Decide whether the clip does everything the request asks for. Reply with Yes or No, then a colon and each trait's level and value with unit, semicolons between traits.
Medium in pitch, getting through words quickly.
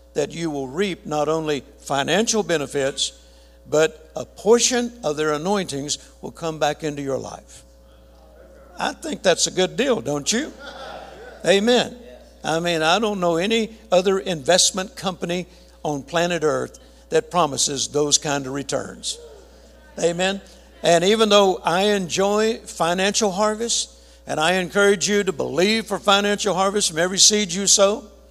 No: medium, 175 Hz; average, 145 wpm